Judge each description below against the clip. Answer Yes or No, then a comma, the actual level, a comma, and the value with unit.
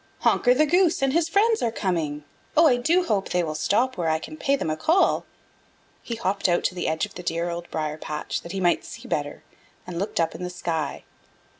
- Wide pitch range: Yes, wide, 8.5 semitones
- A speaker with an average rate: No, fast, 235 wpm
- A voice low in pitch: No, medium, 185 Hz